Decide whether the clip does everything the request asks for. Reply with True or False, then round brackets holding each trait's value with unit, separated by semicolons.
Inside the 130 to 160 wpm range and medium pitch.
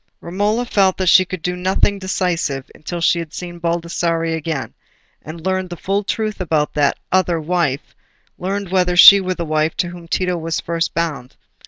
False (175 wpm; 175 Hz)